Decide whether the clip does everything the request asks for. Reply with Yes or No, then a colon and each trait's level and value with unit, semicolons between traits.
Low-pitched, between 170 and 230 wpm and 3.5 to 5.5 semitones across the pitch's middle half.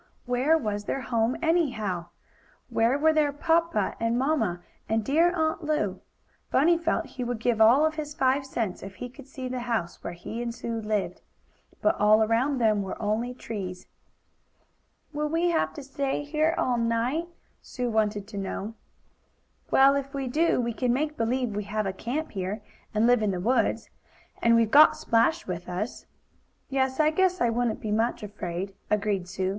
No: high, 240 Hz; average, 180 wpm; average, 5.2 semitones